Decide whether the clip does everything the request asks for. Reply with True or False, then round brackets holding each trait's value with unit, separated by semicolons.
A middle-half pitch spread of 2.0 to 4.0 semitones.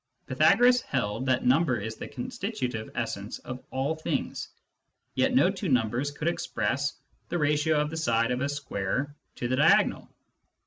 False (4.4 semitones)